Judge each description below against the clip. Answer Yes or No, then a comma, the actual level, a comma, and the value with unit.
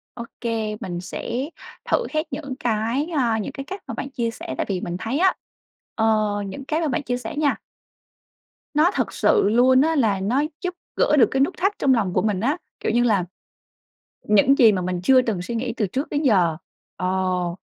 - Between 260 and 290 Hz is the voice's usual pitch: No, high, 235 Hz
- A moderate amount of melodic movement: No, wide, 5.7 semitones